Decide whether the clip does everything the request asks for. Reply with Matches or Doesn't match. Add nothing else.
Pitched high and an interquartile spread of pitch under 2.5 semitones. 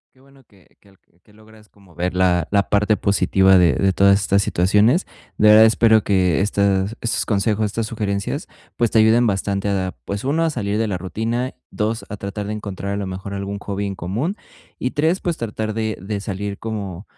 Doesn't match